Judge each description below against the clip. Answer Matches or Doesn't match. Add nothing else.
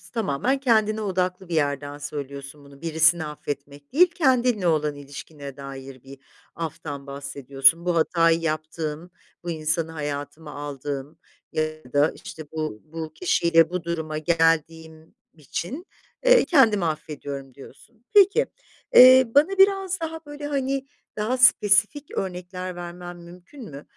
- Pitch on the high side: Doesn't match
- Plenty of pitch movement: Matches